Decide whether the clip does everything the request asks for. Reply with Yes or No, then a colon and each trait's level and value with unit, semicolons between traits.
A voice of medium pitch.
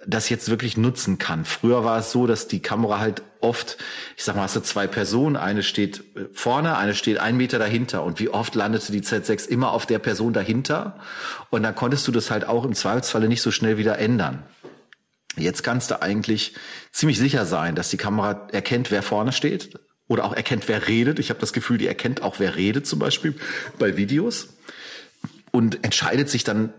No: low, 110 Hz